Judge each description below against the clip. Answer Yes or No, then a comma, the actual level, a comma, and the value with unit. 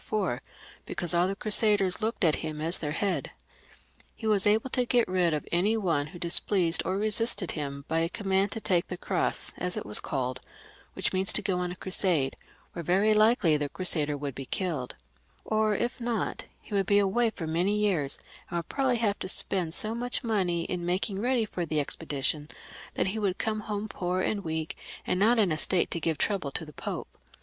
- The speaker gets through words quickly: Yes, fast, 210 wpm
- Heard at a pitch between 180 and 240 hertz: Yes, medium, 185 Hz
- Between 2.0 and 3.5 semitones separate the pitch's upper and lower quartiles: No, average, 4.5 semitones